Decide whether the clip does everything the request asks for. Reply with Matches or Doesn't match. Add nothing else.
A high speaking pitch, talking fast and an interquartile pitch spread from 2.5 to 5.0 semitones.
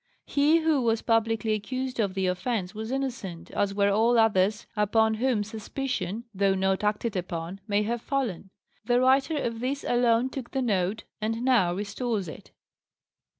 Doesn't match